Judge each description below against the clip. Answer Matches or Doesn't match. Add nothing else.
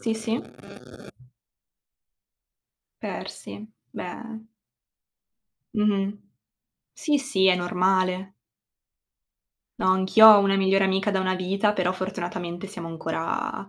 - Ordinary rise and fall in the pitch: Doesn't match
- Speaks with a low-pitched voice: Doesn't match